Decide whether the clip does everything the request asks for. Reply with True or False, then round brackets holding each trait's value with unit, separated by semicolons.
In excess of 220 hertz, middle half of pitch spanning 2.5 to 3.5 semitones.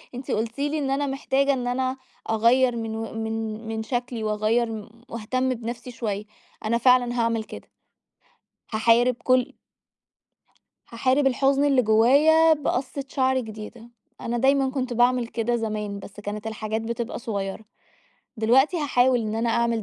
True (235 Hz; 2.8 semitones)